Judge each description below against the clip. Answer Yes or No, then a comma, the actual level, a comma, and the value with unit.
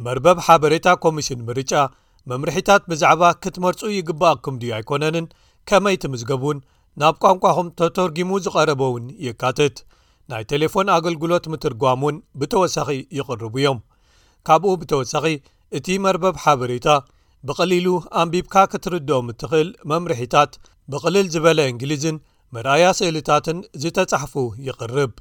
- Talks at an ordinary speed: Yes, average, 100 wpm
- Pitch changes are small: No, average, 4.9 semitones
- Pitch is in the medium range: Yes, medium, 155 Hz